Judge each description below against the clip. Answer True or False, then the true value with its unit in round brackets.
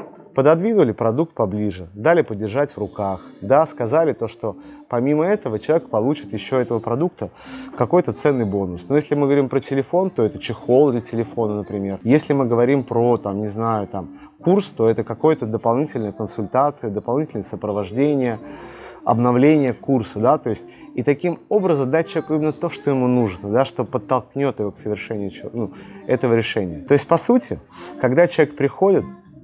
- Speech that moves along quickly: True (165 wpm)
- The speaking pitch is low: True (130 Hz)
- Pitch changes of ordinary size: False (5.7 semitones)